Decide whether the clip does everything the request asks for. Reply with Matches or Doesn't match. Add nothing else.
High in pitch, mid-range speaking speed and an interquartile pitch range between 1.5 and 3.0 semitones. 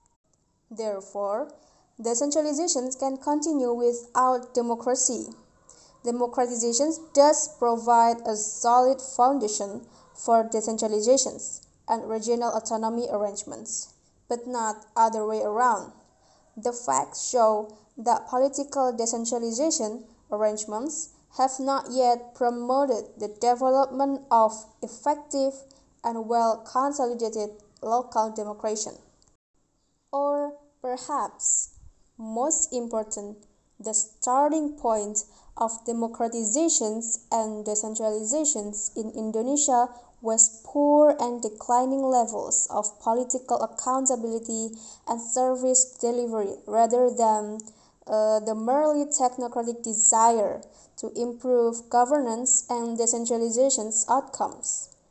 Doesn't match